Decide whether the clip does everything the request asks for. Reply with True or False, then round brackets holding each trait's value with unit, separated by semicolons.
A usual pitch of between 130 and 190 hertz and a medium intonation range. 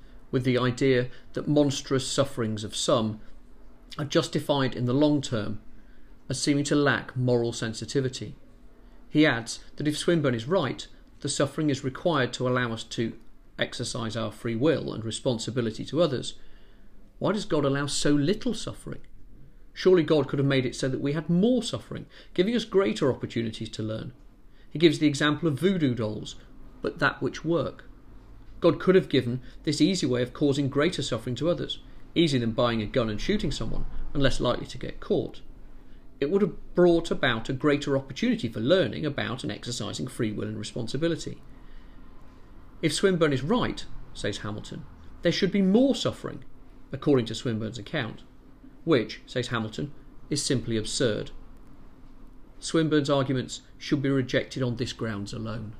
True (135 Hz; 4.6 semitones)